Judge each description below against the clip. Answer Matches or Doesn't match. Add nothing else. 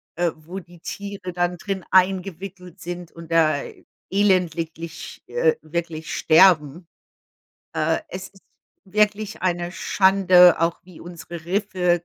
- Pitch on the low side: Doesn't match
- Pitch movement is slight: Matches